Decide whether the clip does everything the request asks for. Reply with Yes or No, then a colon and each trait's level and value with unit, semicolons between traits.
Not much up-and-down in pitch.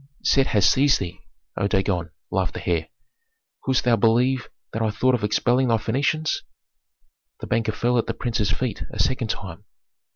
No: average, 3.7 semitones